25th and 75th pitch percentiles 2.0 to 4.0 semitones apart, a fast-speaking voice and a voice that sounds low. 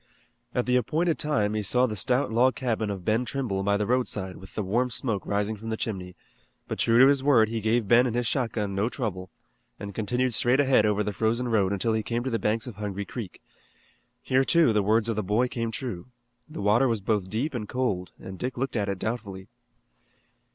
Yes: average, 3.5 semitones; fast, 220 wpm; low, 110 Hz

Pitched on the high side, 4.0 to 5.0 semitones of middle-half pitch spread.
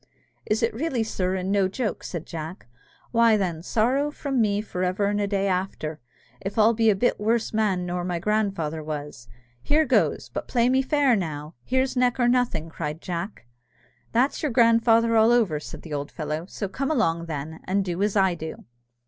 No: high, 200 Hz; wide, 5.5 semitones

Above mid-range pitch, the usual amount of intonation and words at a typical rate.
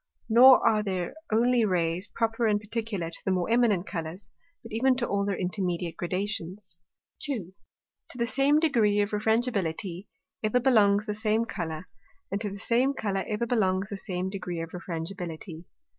Yes: high, 205 Hz; average, 4.0 semitones; average, 165 wpm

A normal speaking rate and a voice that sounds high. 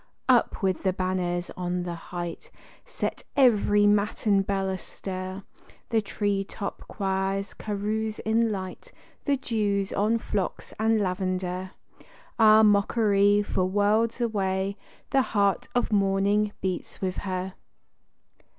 No: slow, 120 wpm; high, 200 Hz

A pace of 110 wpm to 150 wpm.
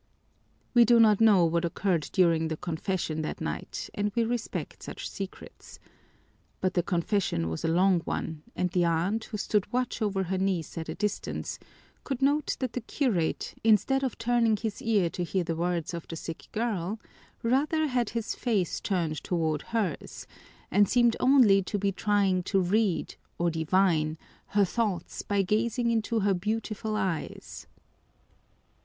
No: average, 160 wpm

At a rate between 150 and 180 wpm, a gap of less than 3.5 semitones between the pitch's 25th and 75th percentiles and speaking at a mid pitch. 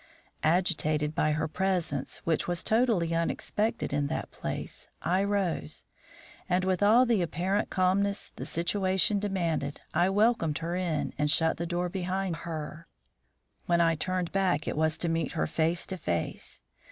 Yes: average, 155 wpm; average, 3.1 semitones; medium, 175 Hz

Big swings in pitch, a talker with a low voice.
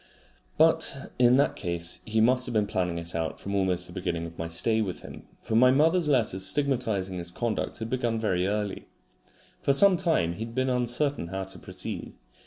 Yes: wide, 6.1 semitones; low, 110 Hz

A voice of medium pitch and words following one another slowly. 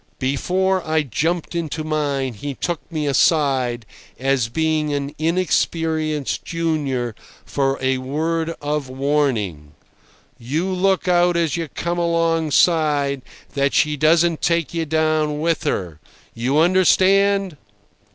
Yes: medium, 155 Hz; slow, 120 wpm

